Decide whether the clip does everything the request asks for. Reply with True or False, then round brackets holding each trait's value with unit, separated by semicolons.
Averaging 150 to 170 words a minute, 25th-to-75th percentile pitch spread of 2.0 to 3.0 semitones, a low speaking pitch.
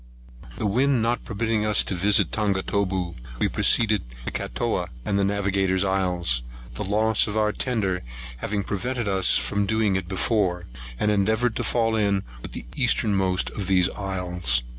True (155 wpm; 2.5 semitones; 100 Hz)